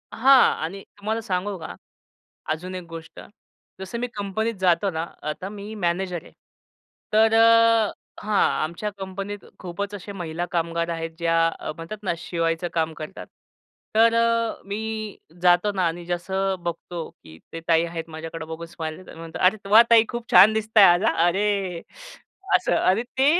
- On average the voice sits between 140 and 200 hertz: Yes, medium, 185 Hz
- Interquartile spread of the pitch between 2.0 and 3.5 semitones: No, average, 4.2 semitones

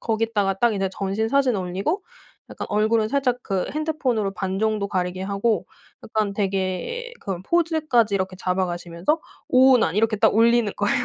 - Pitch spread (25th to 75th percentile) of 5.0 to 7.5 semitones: No, average, 4.2 semitones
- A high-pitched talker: Yes, high, 215 Hz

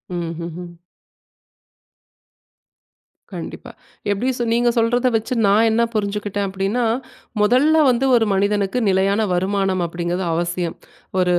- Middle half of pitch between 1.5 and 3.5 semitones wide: No, average, 4.1 semitones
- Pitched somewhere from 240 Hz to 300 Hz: No, high, 200 Hz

